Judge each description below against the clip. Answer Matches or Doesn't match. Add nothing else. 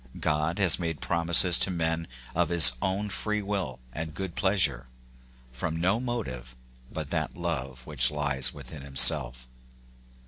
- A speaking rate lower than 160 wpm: Matches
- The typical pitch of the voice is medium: Doesn't match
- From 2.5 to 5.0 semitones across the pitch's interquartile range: Doesn't match